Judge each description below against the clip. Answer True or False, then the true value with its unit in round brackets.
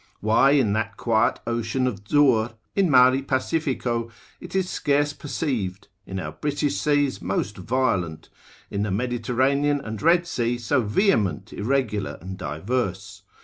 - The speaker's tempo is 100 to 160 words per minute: True (140 wpm)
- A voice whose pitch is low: True (120 Hz)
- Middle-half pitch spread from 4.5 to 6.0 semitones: True (5.2 semitones)